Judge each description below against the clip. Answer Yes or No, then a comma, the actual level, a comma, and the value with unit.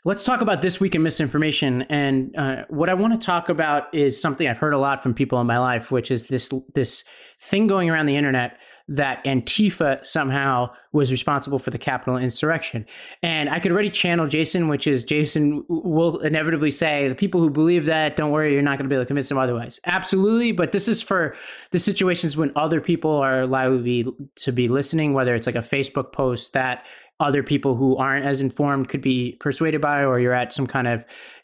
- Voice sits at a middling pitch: Yes, medium, 145 Hz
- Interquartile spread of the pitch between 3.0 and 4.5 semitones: Yes, average, 3.7 semitones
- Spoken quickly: Yes, fast, 215 wpm